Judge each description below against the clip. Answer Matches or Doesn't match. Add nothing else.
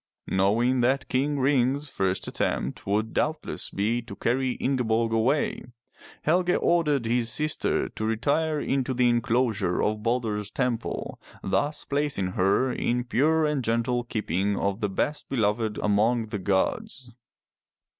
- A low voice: Matches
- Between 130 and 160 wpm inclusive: Matches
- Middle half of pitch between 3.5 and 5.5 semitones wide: Matches